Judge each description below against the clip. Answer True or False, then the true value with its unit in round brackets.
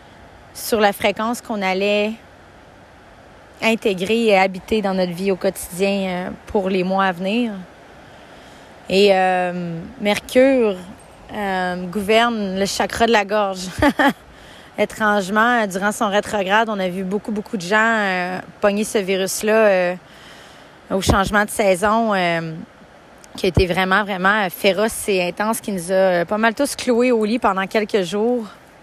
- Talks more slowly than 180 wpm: True (145 wpm)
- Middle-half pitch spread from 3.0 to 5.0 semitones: False (2.6 semitones)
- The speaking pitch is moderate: False (205 Hz)